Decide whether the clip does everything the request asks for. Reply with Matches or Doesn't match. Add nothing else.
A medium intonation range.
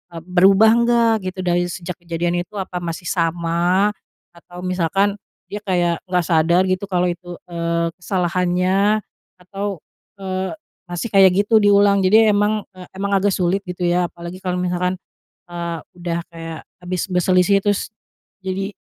Doesn't match